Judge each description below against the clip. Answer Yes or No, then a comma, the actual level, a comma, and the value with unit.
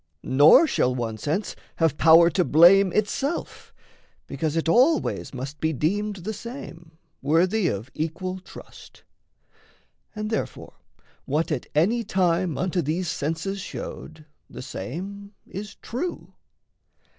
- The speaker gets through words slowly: Yes, slow, 120 wpm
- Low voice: No, medium, 170 Hz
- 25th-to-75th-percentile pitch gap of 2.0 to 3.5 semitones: No, average, 4.6 semitones